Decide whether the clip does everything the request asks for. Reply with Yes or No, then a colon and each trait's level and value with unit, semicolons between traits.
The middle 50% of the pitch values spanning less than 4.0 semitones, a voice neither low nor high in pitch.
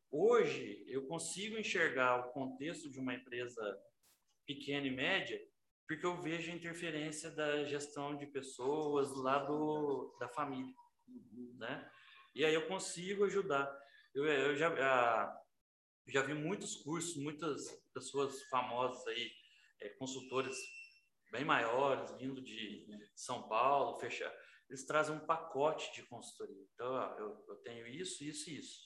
No: average, 5.3 semitones; medium, 150 Hz